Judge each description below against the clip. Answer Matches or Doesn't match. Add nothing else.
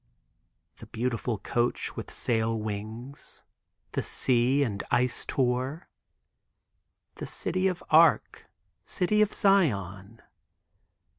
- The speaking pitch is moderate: Doesn't match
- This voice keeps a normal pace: Doesn't match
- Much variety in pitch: Matches